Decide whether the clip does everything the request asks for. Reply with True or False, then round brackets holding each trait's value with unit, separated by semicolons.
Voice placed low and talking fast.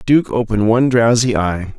False (115 Hz; 170 wpm)